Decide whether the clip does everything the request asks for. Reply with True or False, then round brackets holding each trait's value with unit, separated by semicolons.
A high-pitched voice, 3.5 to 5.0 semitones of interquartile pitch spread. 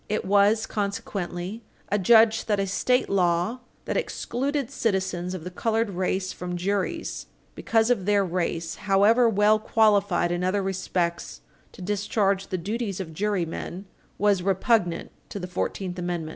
False (195 Hz; 3.1 semitones)